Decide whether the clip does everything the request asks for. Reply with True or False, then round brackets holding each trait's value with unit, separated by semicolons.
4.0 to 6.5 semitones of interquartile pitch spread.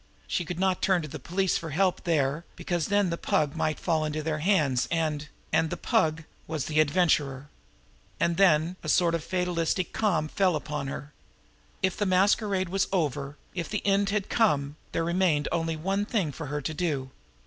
False (3.6 semitones)